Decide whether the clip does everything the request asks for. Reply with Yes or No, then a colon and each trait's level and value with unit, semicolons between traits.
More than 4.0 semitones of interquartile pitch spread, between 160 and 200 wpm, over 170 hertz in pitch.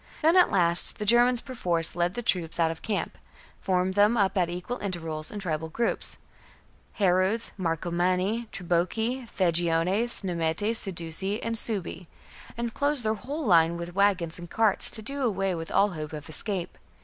Yes: average, 4.6 semitones; average, 170 wpm; high, 190 Hz